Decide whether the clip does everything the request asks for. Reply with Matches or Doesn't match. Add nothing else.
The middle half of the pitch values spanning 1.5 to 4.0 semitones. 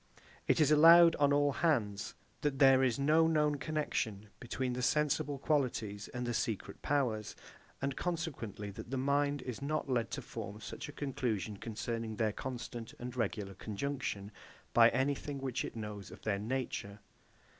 Doesn't match